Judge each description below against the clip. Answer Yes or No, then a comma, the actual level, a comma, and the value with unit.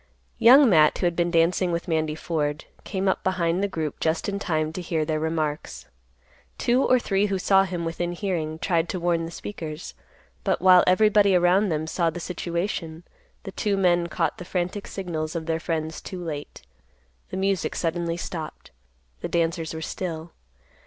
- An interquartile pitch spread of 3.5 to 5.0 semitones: No, average, 2.8 semitones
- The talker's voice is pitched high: No, medium, 170 Hz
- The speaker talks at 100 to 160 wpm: No, average, 180 wpm